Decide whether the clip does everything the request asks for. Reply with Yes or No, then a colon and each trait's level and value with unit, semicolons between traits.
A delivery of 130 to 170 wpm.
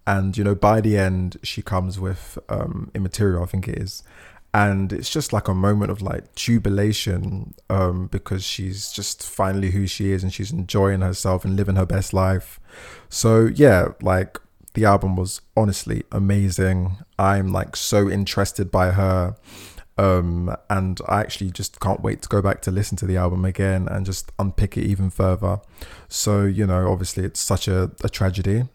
No: average, 180 wpm